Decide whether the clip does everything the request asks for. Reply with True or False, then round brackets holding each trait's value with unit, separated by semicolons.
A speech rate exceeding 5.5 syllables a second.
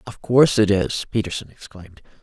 True (6.0 syllables/s)